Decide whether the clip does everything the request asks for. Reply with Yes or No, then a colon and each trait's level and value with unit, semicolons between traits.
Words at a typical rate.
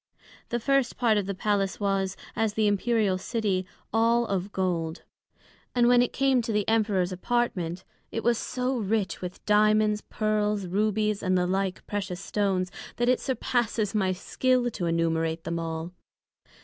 Yes: average, 160 wpm